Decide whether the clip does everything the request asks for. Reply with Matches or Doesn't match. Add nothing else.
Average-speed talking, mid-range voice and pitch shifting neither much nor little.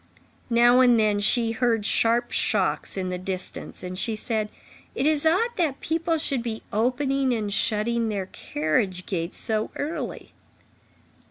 Doesn't match